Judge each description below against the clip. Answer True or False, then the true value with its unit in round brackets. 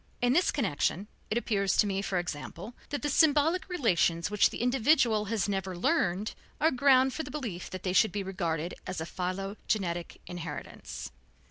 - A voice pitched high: True (205 Hz)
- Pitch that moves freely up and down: True (6.1 semitones)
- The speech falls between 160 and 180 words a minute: True (170 wpm)